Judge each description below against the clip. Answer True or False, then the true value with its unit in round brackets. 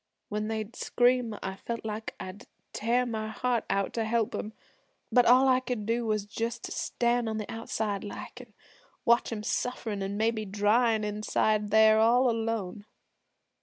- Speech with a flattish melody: True (2.0 semitones)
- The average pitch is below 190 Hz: False (220 Hz)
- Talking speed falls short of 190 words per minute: True (165 wpm)